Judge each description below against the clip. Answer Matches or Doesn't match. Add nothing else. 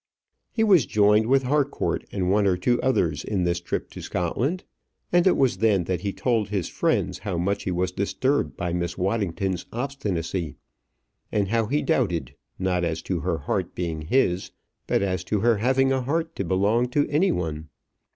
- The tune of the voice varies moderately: Doesn't match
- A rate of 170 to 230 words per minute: Matches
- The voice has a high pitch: Doesn't match